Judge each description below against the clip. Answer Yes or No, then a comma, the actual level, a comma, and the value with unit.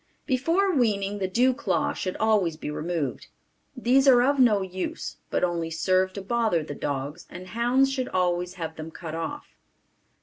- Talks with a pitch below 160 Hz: No, high, 190 Hz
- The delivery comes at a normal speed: Yes, average, 170 wpm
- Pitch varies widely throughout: Yes, wide, 6.6 semitones